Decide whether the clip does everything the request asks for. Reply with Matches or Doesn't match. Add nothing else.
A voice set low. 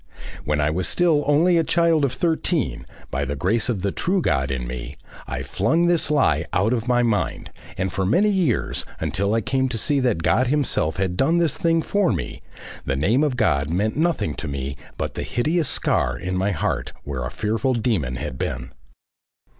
Matches